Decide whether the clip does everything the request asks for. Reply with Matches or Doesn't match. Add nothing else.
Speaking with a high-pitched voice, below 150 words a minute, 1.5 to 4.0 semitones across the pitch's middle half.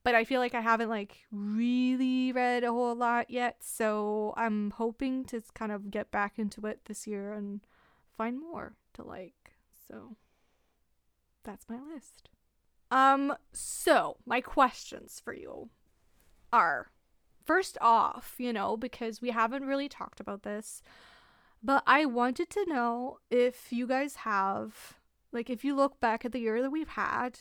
Doesn't match